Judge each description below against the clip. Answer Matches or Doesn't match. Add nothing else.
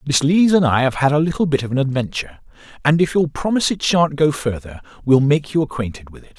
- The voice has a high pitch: Doesn't match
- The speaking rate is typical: Doesn't match